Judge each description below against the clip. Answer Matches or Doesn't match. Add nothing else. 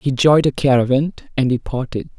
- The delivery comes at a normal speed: Matches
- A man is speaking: Matches